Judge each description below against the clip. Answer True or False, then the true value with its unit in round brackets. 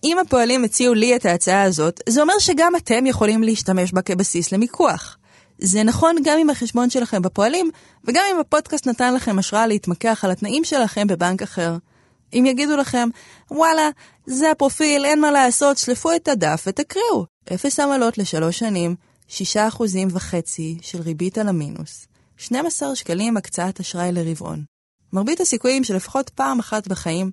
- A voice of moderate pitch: False (225 Hz)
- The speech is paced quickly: True (155 wpm)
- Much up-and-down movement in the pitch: True (7.2 semitones)